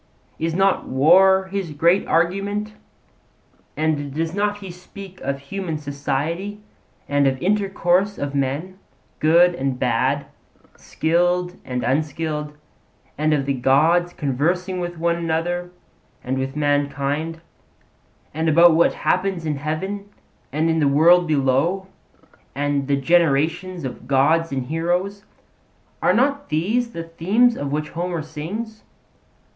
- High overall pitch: No, medium, 165 Hz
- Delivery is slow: Yes, slow, 130 wpm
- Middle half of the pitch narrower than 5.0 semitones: Yes, average, 4.2 semitones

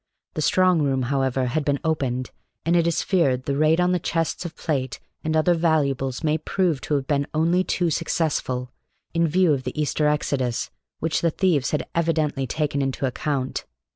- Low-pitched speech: No, medium, 150 Hz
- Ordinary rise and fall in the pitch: Yes, average, 3.6 semitones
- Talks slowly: No, average, 185 wpm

